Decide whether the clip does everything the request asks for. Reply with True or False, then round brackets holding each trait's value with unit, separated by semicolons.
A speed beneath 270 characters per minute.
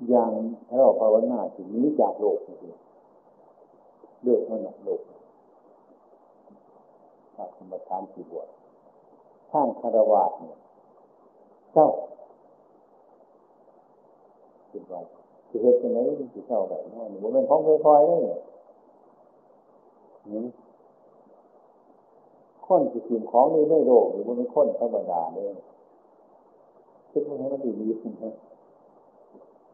False (300 characters per minute)